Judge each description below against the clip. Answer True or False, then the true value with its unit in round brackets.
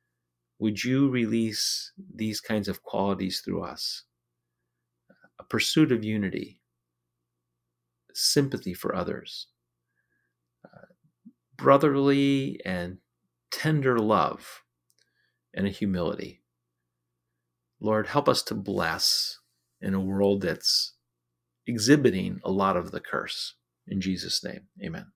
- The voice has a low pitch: True (90 Hz)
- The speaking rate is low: True (105 wpm)